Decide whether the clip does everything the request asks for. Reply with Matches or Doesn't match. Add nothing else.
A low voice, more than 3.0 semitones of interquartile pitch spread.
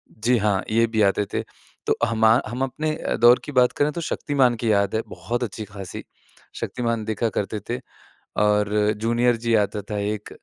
Doesn't match